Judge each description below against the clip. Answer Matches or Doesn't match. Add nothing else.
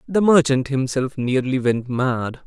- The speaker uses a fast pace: Doesn't match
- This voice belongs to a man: Matches